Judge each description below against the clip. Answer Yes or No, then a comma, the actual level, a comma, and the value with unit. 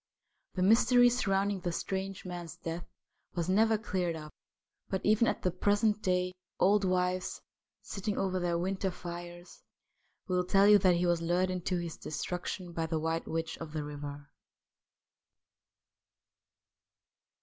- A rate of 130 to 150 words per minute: Yes, average, 140 wpm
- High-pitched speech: No, medium, 180 Hz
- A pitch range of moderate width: No, narrow, 2.3 semitones